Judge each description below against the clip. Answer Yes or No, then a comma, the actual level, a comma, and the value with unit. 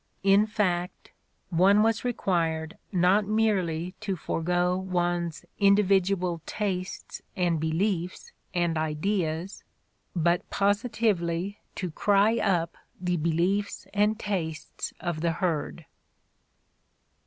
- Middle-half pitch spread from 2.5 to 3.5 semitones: Yes, average, 3.1 semitones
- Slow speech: Yes, slow, 95 wpm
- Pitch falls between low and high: Yes, medium, 180 Hz